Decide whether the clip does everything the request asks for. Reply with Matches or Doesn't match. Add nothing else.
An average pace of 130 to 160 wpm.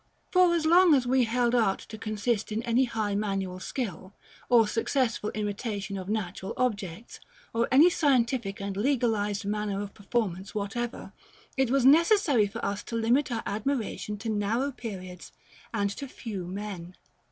Matches